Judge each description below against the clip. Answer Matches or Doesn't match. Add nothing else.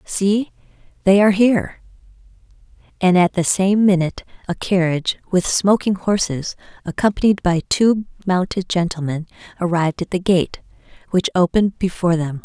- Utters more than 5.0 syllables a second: Matches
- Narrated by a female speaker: Matches